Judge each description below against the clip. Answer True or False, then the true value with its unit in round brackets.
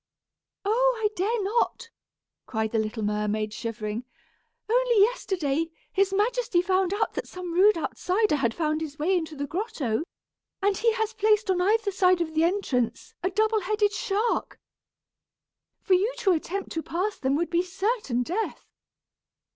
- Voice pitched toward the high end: True (375 Hz)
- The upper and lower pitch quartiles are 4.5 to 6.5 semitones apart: True (5.6 semitones)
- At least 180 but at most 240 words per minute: False (155 wpm)